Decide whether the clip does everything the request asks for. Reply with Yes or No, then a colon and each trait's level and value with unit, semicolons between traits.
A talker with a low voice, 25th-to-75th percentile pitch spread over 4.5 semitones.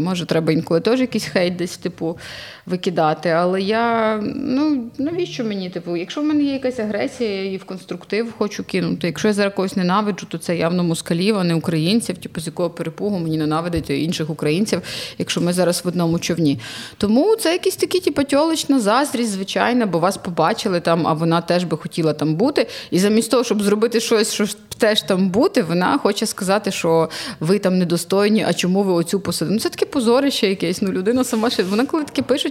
No: high, 195 Hz; average, 5.1 semitones